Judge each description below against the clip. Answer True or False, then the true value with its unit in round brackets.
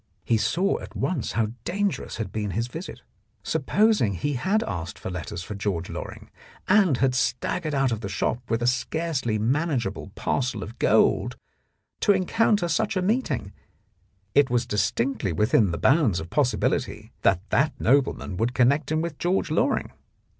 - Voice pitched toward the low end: True (130 Hz)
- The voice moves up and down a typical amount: False (7.7 semitones)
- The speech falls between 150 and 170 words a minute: True (160 wpm)